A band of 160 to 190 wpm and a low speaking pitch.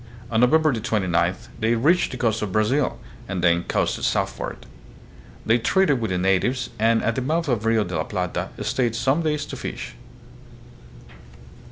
Yes: average, 170 wpm; low, 115 Hz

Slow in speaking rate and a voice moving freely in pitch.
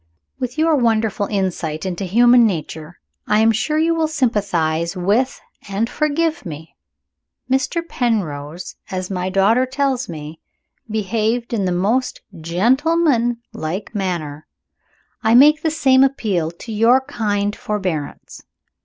Yes: slow, 125 wpm; wide, 6.3 semitones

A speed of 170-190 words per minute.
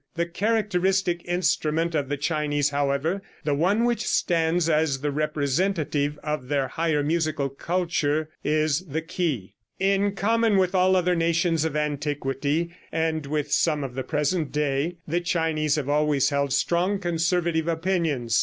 No: average, 150 wpm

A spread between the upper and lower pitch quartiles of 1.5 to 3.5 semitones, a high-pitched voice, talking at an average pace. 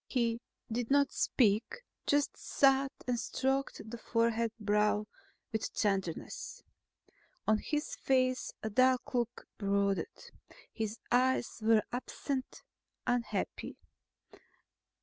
No: average, 3.2 semitones; high, 235 Hz; slow, 100 wpm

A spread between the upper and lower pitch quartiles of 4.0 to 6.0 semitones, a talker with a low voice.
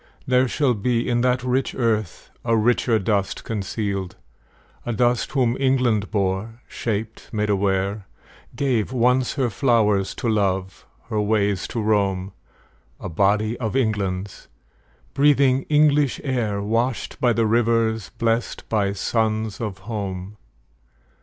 No: average, 3.4 semitones; low, 110 Hz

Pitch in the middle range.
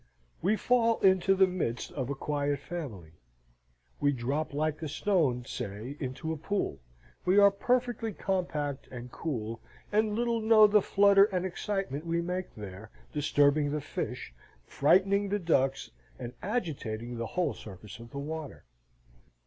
Yes: medium, 155 Hz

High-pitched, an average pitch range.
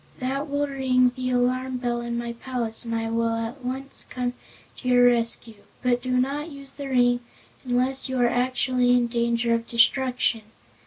No: very high, 250 Hz; narrow, 1.6 semitones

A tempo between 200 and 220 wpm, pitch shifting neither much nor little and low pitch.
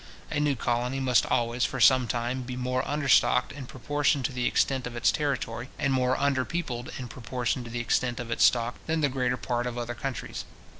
No: fast, 205 wpm; narrow, 2.0 semitones; low, 125 Hz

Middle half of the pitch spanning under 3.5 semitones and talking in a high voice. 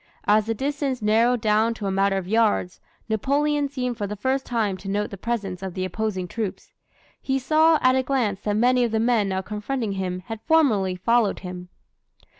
No: average, 4.3 semitones; high, 220 Hz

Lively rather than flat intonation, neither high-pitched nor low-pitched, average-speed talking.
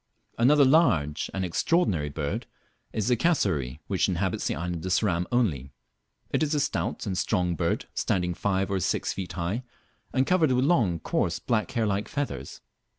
No: wide, 6.6 semitones; very low, 95 Hz; average, 170 wpm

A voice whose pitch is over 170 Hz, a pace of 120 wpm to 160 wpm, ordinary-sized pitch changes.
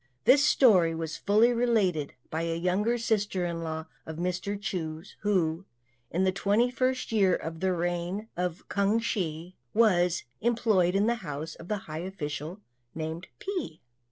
Yes: medium, 185 Hz; average, 155 wpm; average, 4.5 semitones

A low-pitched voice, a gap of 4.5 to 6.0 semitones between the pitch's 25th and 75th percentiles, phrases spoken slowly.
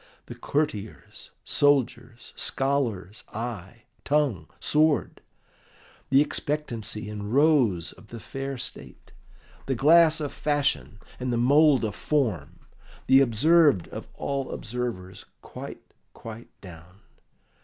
Yes: low, 125 Hz; average, 5.3 semitones; slow, 110 wpm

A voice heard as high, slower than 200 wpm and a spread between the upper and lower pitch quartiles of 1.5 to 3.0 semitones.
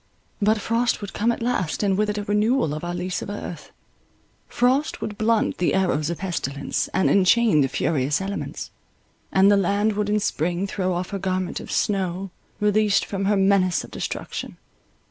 Yes: high, 195 Hz; average, 185 wpm; average, 2.7 semitones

